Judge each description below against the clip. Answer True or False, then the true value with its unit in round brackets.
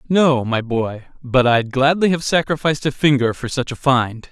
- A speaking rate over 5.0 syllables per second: False (4.9 syllables/s)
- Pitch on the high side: False (135 Hz)